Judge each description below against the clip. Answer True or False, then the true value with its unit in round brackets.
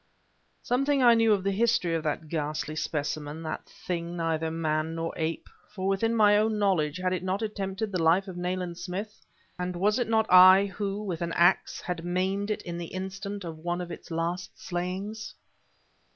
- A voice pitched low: False (185 Hz)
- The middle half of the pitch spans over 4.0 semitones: False (3.4 semitones)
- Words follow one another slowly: False (190 wpm)